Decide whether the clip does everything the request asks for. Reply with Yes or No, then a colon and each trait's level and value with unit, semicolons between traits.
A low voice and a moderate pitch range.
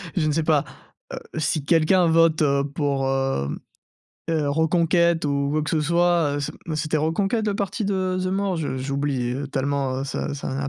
No: medium, 155 Hz; average, 3.4 semitones